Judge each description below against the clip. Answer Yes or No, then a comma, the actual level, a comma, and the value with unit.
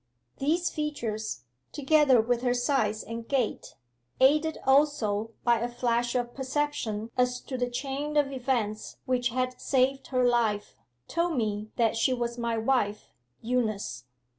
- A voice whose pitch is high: Yes, high, 245 Hz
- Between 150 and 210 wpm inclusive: No, average, 140 wpm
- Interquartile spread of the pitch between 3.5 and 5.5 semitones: No, average, 3.0 semitones